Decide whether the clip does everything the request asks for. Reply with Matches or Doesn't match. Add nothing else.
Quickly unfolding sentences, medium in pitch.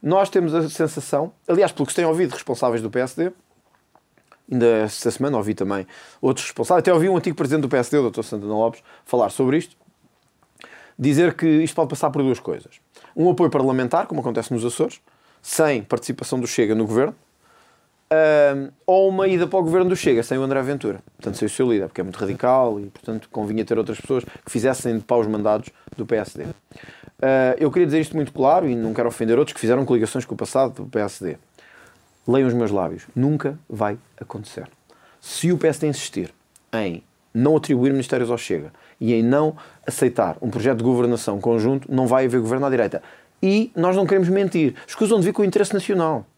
Doesn't match